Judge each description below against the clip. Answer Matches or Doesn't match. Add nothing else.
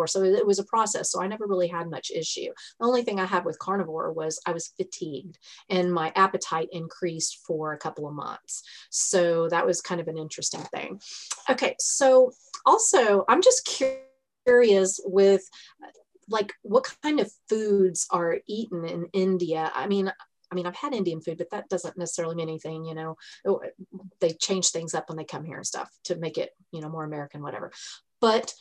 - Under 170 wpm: Doesn't match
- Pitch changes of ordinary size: Matches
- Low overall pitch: Doesn't match